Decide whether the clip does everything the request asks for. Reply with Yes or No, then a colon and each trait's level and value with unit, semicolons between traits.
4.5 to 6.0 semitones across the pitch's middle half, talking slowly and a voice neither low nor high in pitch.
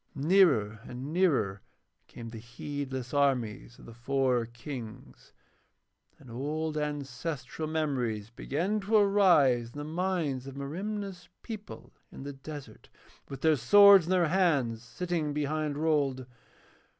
Yes: average, 5.0 semitones; slow, 125 wpm; medium, 145 Hz